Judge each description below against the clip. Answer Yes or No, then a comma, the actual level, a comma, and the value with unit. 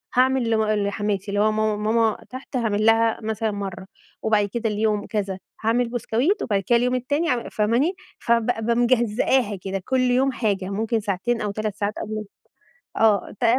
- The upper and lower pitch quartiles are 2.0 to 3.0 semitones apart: Yes, narrow, 2.6 semitones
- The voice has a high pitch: Yes, high, 220 Hz